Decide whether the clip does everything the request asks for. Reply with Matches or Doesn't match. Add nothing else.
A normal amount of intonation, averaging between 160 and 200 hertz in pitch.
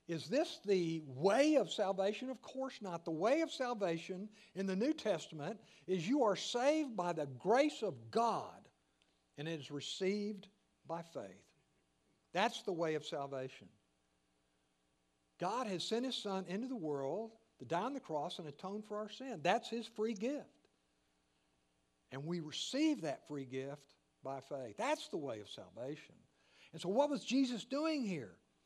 Doesn't match